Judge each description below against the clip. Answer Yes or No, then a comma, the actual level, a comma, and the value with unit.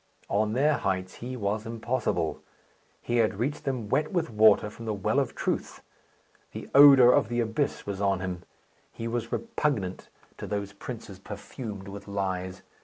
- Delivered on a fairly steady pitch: No, average, 3.7 semitones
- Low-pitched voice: Yes, low, 110 Hz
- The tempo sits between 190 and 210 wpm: No, average, 165 wpm